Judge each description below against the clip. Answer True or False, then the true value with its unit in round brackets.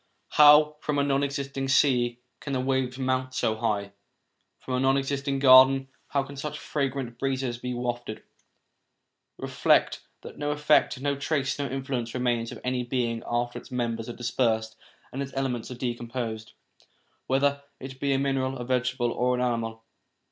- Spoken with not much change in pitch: True (2.2 semitones)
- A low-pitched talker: True (130 Hz)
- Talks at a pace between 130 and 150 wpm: False (170 wpm)